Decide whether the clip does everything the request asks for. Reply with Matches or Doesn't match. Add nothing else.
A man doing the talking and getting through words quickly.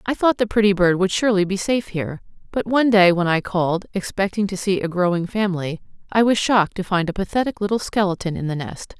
Doesn't match